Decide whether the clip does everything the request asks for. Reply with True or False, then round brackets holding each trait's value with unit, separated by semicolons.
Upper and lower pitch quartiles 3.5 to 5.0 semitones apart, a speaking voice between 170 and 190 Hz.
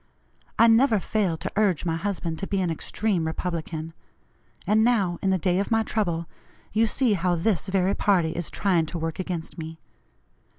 True (4.0 semitones; 185 Hz)